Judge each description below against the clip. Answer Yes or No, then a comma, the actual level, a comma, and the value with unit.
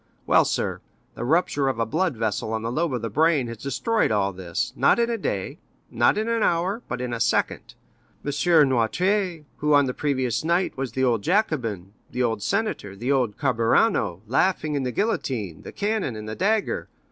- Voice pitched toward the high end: No, low, 135 Hz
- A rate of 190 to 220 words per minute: Yes, average, 195 wpm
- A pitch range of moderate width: No, wide, 7.4 semitones